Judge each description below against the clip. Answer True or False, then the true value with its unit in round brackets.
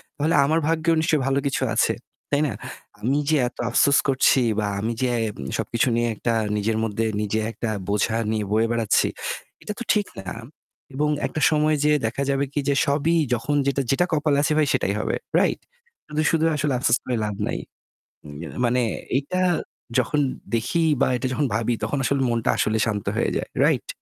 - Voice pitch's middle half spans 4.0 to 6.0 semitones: True (4.8 semitones)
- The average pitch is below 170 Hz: True (135 Hz)